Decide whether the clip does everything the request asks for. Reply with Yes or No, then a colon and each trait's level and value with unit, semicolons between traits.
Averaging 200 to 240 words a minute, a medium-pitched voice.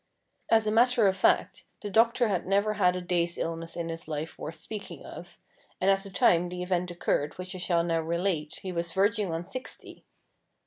Yes: fast, 205 wpm; medium, 180 Hz